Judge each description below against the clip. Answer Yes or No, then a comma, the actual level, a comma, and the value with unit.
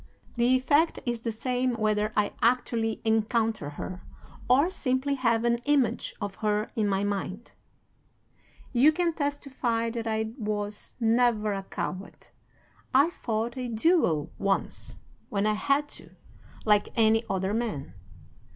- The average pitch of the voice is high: Yes, high, 225 Hz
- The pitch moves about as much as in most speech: Yes, average, 3.2 semitones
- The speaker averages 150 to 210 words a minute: No, slow, 135 wpm